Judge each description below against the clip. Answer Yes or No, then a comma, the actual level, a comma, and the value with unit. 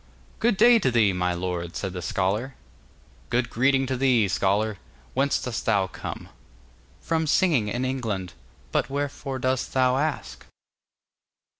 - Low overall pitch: Yes, low, 125 Hz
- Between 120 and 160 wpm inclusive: Yes, average, 140 wpm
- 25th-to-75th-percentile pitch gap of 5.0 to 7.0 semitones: Yes, wide, 5.5 semitones